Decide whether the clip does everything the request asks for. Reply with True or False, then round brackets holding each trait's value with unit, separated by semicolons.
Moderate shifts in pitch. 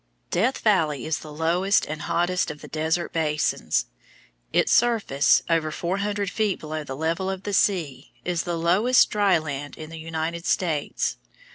True (3.7 semitones)